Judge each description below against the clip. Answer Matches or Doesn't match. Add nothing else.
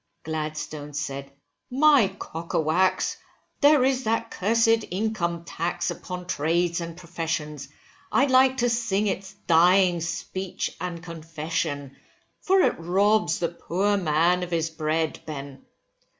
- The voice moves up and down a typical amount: Matches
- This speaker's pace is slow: Matches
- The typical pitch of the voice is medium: Matches